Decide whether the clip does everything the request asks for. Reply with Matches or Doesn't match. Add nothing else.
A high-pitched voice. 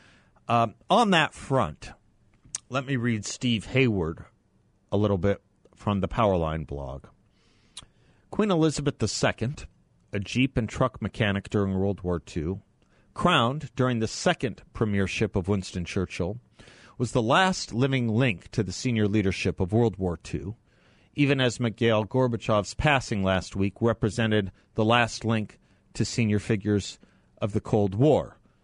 Doesn't match